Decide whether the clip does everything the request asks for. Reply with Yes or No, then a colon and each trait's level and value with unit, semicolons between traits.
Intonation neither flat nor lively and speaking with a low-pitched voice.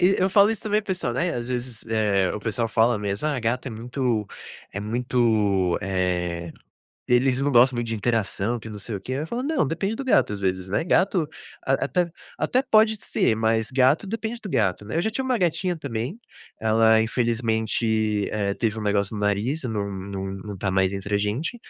No: wide, 6.7 semitones; low, 115 Hz